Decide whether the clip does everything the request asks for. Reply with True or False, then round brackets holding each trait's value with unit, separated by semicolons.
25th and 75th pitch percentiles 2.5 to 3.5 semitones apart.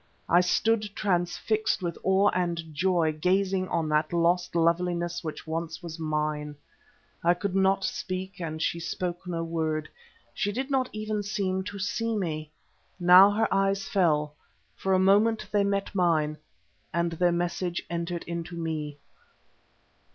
True (2.8 semitones)